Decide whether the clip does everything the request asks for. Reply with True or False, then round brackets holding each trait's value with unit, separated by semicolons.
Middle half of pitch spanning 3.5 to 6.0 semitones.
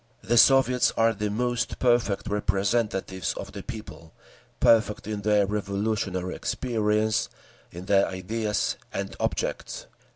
False (2.5 semitones)